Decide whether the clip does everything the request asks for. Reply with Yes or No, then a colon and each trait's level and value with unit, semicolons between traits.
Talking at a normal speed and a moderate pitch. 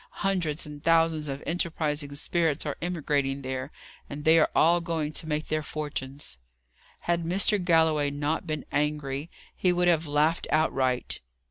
Yes: average, 155 wpm; medium, 155 Hz